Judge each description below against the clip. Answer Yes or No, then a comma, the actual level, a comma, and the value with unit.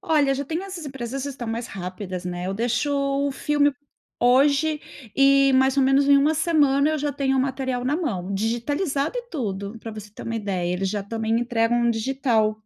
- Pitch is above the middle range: Yes, very high, 260 Hz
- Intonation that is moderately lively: Yes, average, 4.1 semitones